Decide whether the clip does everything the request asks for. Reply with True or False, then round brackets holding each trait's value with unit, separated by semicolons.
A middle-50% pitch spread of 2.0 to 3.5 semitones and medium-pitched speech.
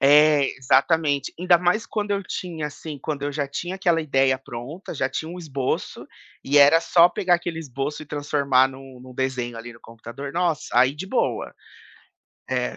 False (4.0 semitones; 145 Hz)